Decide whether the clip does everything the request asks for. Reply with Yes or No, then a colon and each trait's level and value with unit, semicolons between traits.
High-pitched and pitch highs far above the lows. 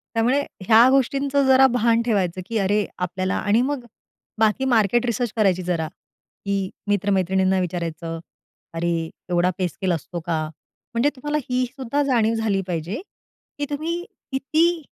Yes: high, 215 Hz; wide, 5.9 semitones